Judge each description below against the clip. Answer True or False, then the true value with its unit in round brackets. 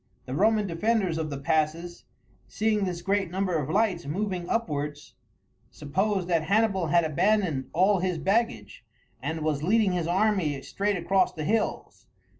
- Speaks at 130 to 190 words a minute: True (150 wpm)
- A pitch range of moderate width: True (4.6 semitones)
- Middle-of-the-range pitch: True (180 Hz)